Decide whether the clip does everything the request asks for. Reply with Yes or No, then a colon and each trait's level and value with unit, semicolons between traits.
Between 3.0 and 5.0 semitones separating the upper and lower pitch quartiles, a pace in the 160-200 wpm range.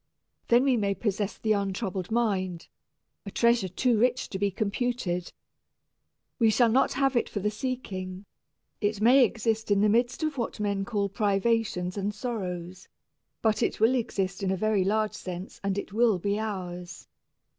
Yes: average, 3.4 semitones; average, 170 wpm